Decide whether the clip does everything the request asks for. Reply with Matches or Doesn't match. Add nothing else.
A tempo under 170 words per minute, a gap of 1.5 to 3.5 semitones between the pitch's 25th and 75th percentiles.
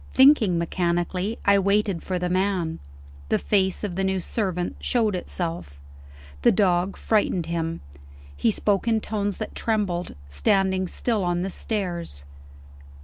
Matches